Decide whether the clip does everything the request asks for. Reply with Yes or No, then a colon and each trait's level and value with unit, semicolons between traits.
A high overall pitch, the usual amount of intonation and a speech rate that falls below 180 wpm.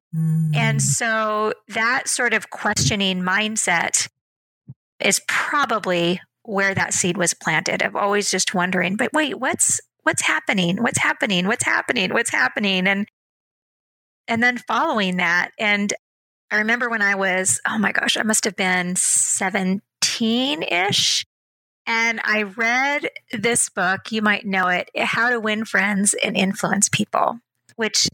Yes: high, 205 Hz; average, 3.6 semitones; average, 140 wpm